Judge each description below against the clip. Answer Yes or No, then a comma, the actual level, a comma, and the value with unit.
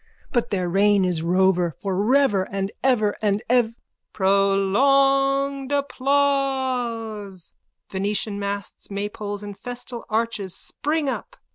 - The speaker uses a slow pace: Yes, slow, 110 wpm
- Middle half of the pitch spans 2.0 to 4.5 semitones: No, average, 5.2 semitones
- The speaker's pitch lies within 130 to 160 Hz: No, high, 210 Hz